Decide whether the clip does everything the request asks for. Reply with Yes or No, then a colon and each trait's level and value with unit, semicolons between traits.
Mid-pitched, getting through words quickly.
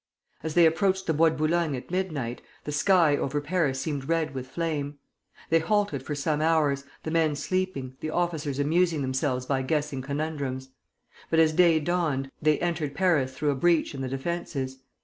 No: medium, 150 Hz; average, 180 wpm